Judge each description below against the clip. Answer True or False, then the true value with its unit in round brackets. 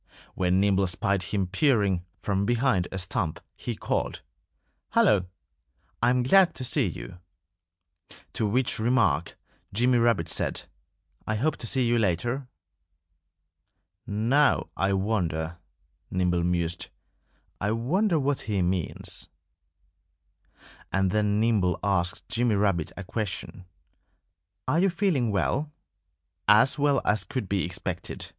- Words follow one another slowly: True (125 wpm)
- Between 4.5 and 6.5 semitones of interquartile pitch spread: True (5.1 semitones)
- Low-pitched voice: True (105 Hz)